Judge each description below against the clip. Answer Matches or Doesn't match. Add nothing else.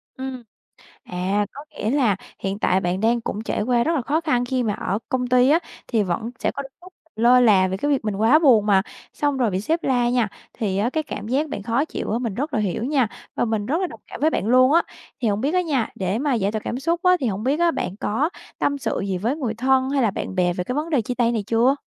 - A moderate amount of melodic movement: Matches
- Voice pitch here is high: Matches